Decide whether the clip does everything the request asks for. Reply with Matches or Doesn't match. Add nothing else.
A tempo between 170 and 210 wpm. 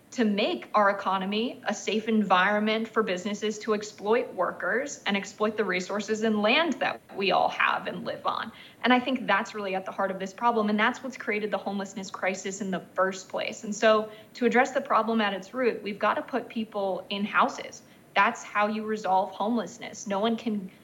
Matches